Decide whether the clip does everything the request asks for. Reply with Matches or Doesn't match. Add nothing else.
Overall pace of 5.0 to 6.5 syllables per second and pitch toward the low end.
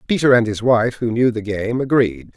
Matches